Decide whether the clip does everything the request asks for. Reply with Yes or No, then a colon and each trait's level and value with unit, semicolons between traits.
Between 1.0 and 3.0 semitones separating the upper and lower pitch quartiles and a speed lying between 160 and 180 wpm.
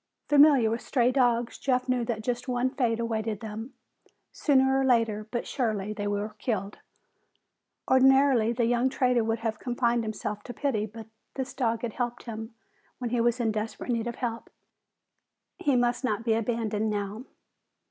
Yes: narrow, 2.4 semitones; average, 170 wpm